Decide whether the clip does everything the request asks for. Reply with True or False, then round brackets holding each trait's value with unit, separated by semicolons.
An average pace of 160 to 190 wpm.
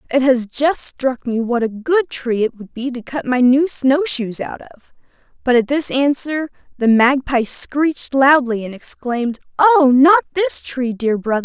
False (205 wpm)